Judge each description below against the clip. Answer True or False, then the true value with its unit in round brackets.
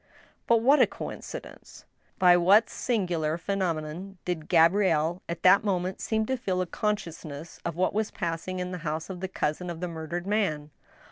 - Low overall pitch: False (180 Hz)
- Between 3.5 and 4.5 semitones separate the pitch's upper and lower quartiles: False (3.1 semitones)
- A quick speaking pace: False (175 wpm)